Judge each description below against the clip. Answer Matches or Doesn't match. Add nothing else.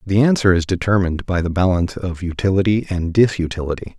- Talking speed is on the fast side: Doesn't match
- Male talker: Matches